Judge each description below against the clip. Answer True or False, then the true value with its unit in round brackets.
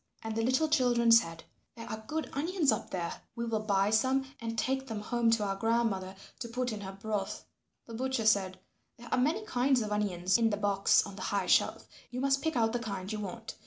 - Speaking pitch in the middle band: False (225 Hz)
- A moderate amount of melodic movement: True (3.7 semitones)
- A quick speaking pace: True (225 wpm)